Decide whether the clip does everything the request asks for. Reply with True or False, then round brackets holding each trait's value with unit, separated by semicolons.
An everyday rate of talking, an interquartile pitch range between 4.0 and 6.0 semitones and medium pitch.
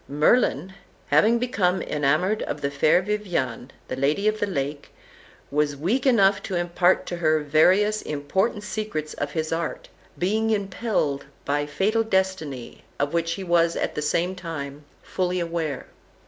True (150 wpm; 5.2 semitones; 170 Hz)